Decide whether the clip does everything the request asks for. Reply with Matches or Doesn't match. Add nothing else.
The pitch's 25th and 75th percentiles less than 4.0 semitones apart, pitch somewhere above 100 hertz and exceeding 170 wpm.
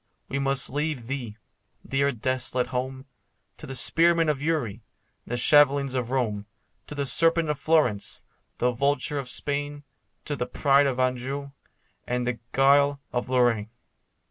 Doesn't match